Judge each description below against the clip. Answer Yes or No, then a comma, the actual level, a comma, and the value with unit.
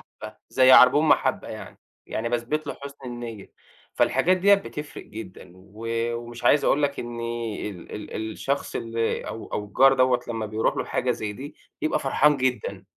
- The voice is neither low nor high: No, low, 120 Hz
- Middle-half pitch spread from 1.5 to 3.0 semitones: No, average, 3.8 semitones